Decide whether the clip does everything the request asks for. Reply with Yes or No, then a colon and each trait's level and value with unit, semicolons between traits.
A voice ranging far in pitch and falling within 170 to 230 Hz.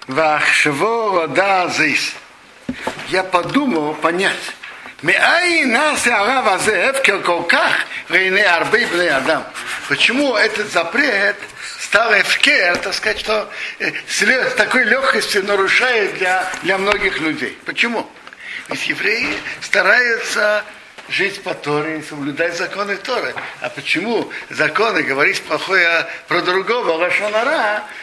No: average, 4.5 semitones; high, 190 Hz